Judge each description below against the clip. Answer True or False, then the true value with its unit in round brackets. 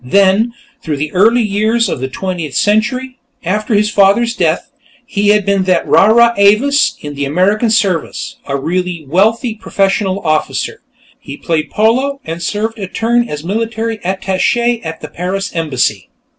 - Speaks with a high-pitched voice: True (200 Hz)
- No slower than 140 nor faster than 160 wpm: True (155 wpm)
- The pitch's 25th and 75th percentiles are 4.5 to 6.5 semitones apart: True (4.8 semitones)